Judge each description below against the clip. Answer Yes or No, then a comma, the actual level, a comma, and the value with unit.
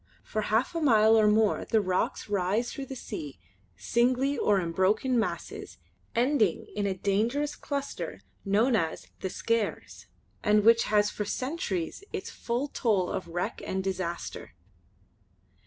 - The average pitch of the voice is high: Yes, high, 215 Hz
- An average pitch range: Yes, average, 4.3 semitones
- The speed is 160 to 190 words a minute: No, average, 150 wpm